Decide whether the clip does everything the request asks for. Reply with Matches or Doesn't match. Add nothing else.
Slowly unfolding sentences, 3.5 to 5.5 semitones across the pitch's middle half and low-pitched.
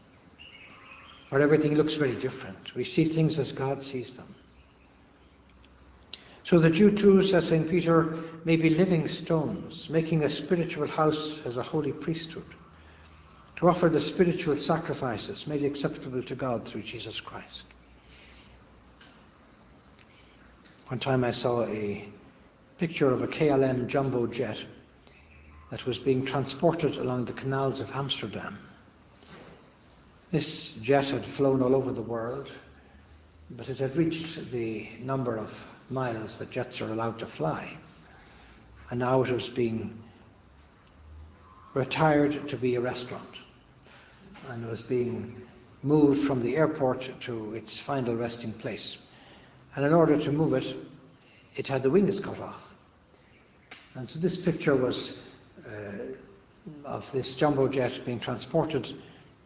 Matches